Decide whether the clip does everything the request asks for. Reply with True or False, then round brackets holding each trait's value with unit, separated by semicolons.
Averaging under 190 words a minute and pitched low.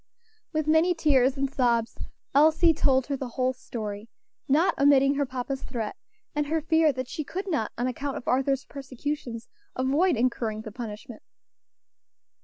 False (155 wpm; 270 Hz)